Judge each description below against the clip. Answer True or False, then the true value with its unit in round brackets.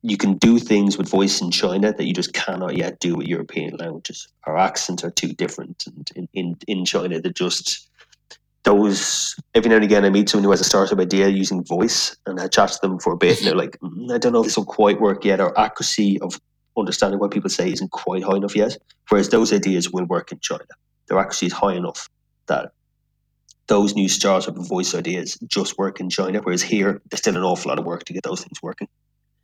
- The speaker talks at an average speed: False (230 wpm)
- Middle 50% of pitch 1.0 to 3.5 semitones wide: True (3.1 semitones)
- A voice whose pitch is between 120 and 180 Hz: False (100 Hz)